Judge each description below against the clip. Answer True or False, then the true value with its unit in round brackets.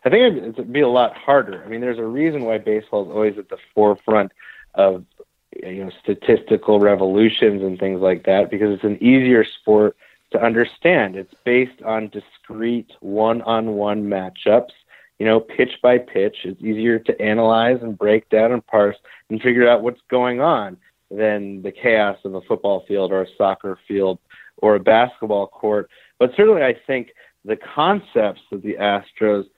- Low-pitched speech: True (105 Hz)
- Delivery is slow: False (175 wpm)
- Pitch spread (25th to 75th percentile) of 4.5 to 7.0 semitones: False (2.8 semitones)